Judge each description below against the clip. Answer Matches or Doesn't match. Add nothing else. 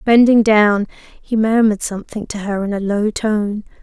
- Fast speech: Doesn't match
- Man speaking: Doesn't match